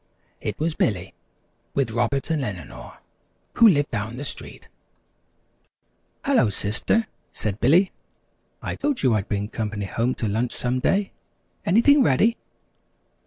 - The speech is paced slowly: Yes, slow, 130 wpm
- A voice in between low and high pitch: No, low, 125 Hz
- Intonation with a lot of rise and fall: Yes, wide, 8.9 semitones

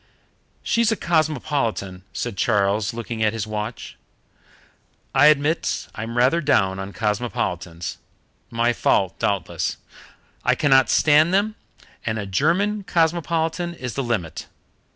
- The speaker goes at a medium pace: No, slow, 120 wpm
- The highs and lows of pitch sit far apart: Yes, wide, 7.2 semitones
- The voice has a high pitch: No, low, 120 Hz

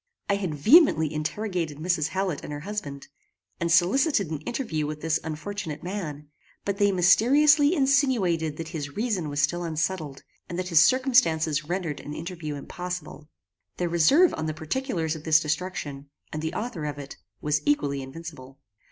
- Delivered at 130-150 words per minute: No, average, 160 wpm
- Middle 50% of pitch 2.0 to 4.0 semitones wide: No, average, 4.8 semitones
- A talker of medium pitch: Yes, medium, 165 Hz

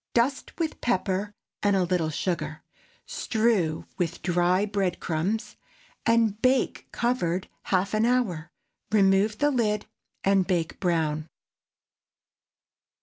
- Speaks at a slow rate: Yes, slow, 110 wpm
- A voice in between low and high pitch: No, high, 195 Hz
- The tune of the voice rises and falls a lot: No, average, 4.2 semitones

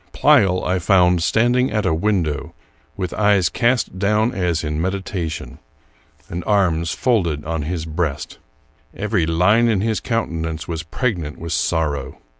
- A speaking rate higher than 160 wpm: No, average, 145 wpm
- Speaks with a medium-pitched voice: No, very low, 90 Hz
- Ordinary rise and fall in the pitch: Yes, average, 4.5 semitones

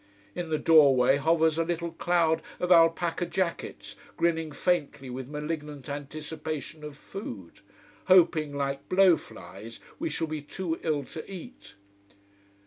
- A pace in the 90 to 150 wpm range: Yes, slow, 135 wpm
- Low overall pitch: No, medium, 160 Hz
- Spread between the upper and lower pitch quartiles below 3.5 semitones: Yes, average, 2.9 semitones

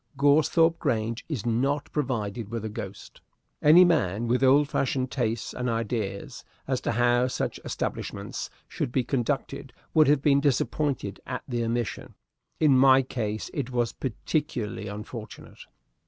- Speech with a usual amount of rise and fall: Yes, average, 3.6 semitones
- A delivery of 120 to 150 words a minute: Yes, average, 140 wpm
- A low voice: Yes, low, 125 Hz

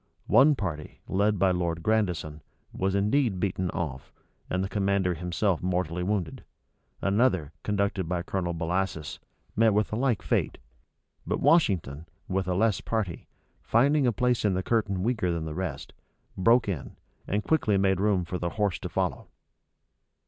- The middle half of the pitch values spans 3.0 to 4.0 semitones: Yes, average, 3.4 semitones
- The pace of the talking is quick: No, average, 155 wpm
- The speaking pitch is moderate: No, very low, 95 Hz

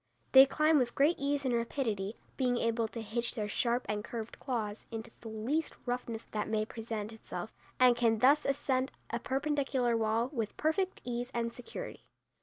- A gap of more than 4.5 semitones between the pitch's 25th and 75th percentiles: No, average, 3.2 semitones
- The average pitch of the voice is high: Yes, high, 240 Hz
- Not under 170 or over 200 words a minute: Yes, average, 175 wpm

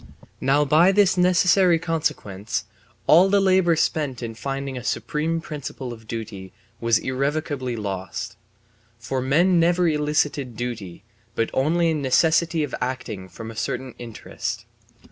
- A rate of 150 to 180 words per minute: No, slow, 135 wpm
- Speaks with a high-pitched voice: No, medium, 140 Hz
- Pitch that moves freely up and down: Yes, wide, 6.0 semitones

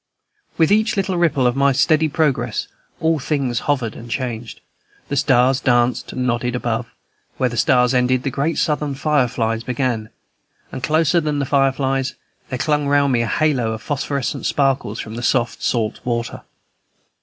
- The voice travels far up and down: No, average, 3.2 semitones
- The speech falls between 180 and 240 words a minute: No, average, 165 wpm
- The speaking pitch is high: No, low, 130 Hz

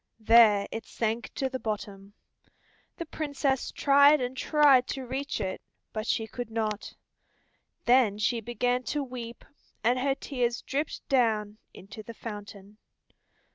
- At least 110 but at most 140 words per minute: Yes, slow, 135 wpm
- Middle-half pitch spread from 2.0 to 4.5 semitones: Yes, average, 3.7 semitones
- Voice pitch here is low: No, high, 240 Hz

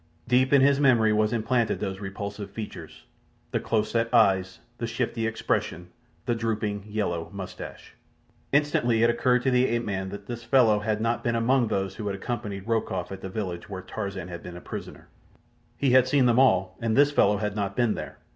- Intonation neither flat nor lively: Yes, average, 3.4 semitones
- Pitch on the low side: Yes, low, 110 Hz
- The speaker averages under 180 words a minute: No, average, 195 wpm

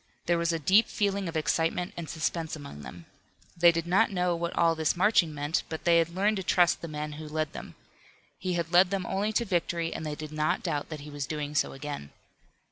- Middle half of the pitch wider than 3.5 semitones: No, average, 2.8 semitones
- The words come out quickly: Yes, fast, 230 wpm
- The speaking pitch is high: No, medium, 165 Hz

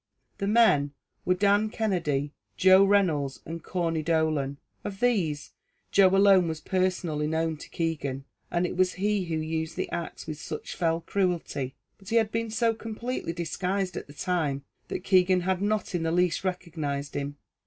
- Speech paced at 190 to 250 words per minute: No, average, 170 wpm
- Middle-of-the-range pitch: Yes, medium, 175 Hz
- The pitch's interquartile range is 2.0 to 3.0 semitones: No, average, 3.7 semitones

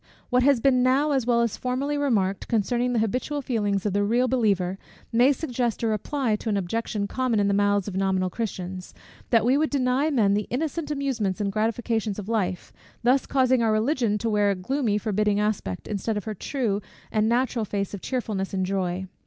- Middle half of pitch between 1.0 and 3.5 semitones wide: No, average, 3.9 semitones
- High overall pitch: Yes, high, 220 Hz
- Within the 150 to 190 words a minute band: No, average, 200 wpm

